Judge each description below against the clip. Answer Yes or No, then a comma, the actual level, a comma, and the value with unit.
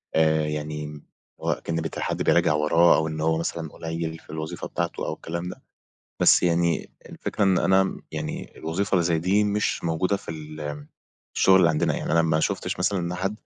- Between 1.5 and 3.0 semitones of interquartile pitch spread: Yes, narrow, 2.5 semitones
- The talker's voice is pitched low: Yes, very low, 80 Hz